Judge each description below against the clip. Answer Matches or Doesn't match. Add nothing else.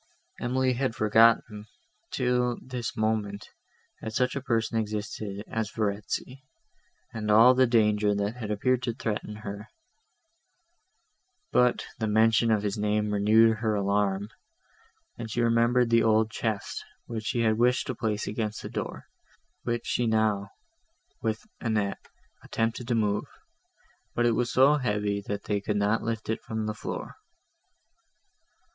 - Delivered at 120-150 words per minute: Matches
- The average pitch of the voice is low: Matches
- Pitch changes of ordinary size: Doesn't match